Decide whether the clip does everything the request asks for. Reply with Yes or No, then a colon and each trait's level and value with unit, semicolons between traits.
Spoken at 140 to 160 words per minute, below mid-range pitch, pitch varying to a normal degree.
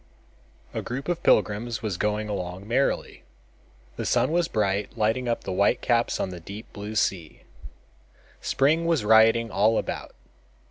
Yes: average, 150 wpm; low, 110 Hz; average, 3.2 semitones